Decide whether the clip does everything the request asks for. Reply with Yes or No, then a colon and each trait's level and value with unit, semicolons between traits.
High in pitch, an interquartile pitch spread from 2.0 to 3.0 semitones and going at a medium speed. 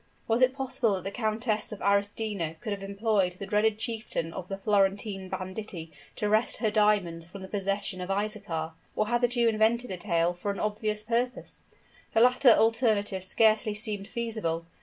Yes: high, 210 Hz; narrow, 2.6 semitones; average, 180 wpm